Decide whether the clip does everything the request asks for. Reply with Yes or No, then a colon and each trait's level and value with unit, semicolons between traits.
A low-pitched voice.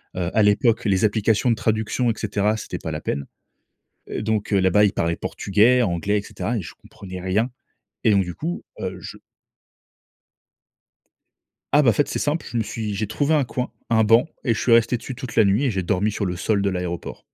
Yes: low, 105 Hz